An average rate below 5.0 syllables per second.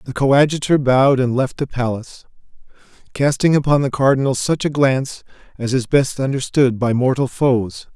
No: 5.3 syllables/s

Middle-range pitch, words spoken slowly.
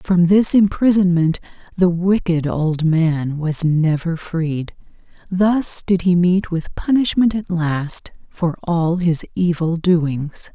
Yes: medium, 170 Hz; slow, 130 wpm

